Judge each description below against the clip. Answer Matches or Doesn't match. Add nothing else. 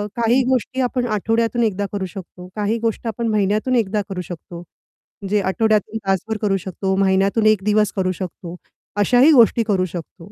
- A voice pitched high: Matches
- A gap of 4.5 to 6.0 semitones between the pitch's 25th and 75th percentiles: Doesn't match